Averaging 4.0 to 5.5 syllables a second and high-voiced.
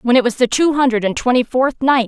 No: 5.9 syllables/s; very high, 250 Hz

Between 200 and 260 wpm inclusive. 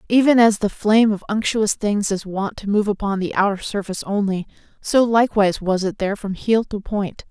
Yes: fast, 205 wpm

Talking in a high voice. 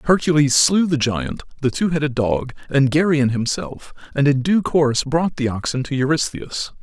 No: medium, 140 Hz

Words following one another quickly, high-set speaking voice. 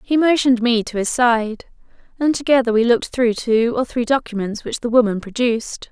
No: average, 195 wpm; high, 240 Hz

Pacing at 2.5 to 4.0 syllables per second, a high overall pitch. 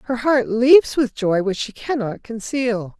Yes: 3.9 syllables/s; high, 235 Hz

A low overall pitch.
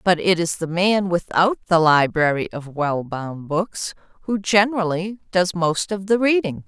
No: medium, 180 Hz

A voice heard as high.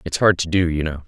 No: very low, 85 Hz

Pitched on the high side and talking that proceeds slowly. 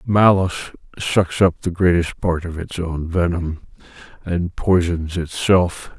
No: very low, 85 Hz; slow, 130 wpm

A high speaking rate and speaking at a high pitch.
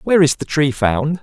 No: fast, 245 wpm; medium, 145 Hz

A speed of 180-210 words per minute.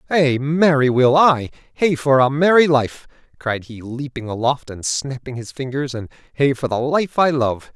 Yes: average, 185 wpm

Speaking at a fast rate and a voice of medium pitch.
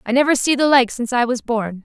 No: fast, 295 wpm; high, 245 Hz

